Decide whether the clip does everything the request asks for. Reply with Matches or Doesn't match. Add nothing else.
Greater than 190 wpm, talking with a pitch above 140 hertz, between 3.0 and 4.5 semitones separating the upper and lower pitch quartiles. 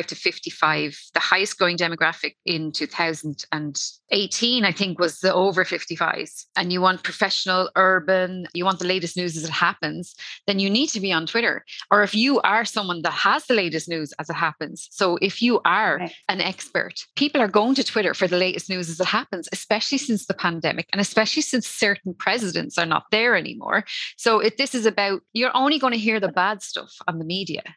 Matches